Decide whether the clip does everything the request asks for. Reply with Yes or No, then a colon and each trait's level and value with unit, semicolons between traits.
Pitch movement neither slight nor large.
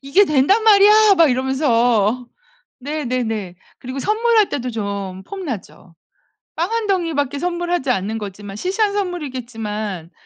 No: wide, 8.7 semitones